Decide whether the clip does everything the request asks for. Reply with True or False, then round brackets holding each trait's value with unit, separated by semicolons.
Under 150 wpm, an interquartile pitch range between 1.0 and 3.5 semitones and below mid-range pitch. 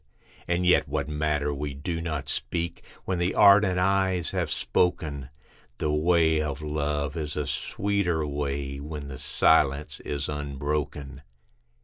True (135 wpm; 3.2 semitones; 75 Hz)